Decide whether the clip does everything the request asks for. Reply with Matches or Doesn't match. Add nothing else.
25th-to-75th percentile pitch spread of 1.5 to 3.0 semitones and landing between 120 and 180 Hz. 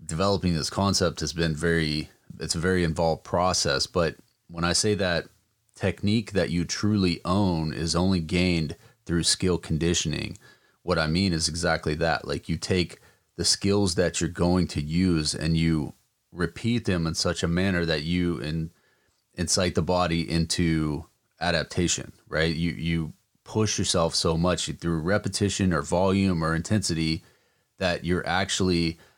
Doesn't match